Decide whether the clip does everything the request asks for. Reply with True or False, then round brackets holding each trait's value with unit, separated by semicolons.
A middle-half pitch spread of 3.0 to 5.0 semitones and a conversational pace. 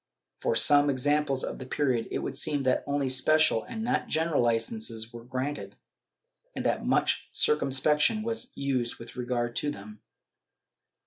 True (3.9 semitones; 155 wpm)